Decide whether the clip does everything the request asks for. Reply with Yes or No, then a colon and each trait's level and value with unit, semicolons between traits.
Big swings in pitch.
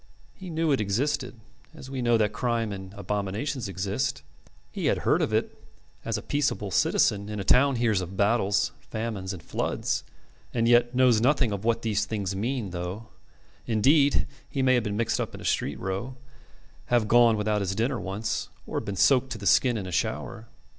No: average, 3.7 semitones